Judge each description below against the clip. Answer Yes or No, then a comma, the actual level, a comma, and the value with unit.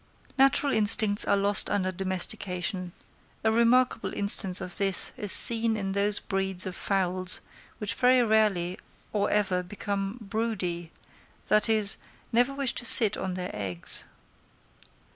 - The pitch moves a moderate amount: Yes, average, 3.0 semitones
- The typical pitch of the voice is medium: No, high, 200 Hz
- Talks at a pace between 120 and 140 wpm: Yes, slow, 135 wpm